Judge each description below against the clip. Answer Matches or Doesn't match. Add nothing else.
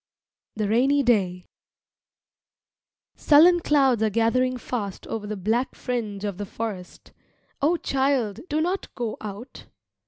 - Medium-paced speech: Doesn't match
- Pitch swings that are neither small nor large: Matches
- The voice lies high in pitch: Matches